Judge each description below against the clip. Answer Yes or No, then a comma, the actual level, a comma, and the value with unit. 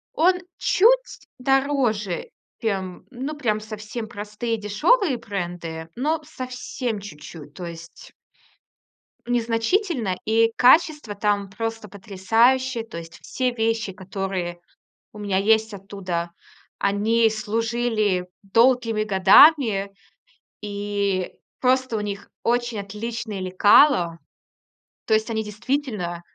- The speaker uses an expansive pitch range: No, average, 3.7 semitones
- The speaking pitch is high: Yes, high, 215 Hz